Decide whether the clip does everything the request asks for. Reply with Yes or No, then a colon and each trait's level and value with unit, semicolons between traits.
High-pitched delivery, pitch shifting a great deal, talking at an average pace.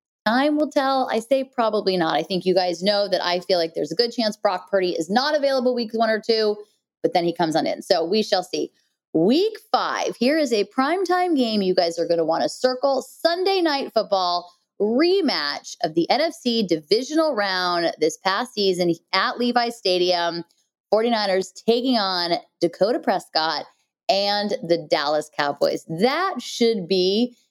Yes: high, 210 Hz; wide, 5.9 semitones; average, 175 wpm